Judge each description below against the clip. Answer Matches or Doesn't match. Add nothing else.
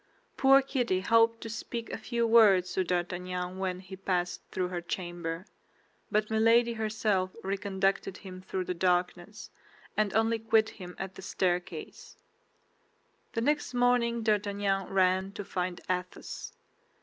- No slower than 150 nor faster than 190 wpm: Doesn't match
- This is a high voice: Matches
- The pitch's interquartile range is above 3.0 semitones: Matches